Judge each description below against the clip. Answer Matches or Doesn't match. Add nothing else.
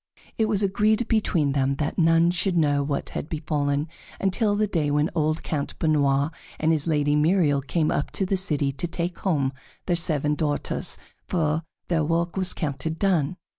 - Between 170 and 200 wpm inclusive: Matches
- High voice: Doesn't match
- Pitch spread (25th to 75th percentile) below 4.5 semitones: Matches